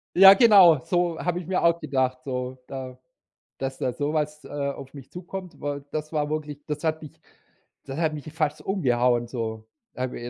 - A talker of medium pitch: Yes, medium, 150 Hz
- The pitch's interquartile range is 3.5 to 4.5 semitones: Yes, average, 4.1 semitones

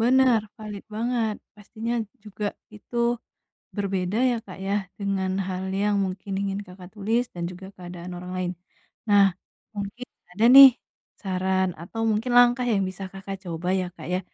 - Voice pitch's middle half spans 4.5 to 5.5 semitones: No, average, 3.0 semitones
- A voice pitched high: Yes, high, 200 Hz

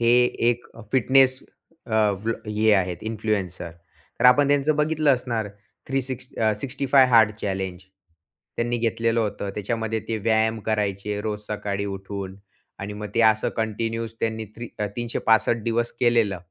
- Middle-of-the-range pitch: No, low, 115 Hz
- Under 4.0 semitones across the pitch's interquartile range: Yes, narrow, 2.5 semitones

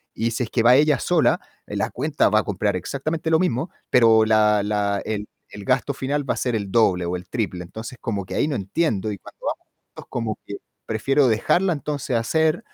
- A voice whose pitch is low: Yes, low, 115 Hz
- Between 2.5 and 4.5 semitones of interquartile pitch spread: No, wide, 5.5 semitones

